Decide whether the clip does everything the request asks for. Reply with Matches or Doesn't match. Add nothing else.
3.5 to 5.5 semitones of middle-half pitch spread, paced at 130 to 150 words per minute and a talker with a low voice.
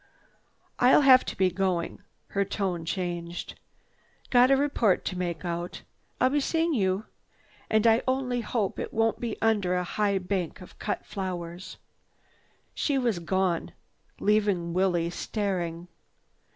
Doesn't match